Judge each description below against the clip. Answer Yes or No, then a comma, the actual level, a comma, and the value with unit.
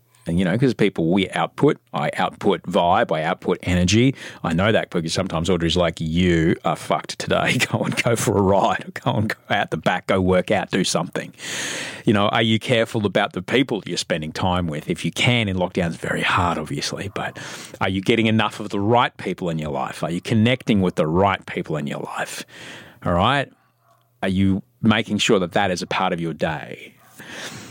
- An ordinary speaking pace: No, fast, 210 wpm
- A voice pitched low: Yes, low, 100 Hz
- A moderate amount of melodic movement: Yes, average, 4.2 semitones